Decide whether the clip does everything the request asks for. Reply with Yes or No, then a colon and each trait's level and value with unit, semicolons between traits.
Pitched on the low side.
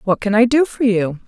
No: high, 225 Hz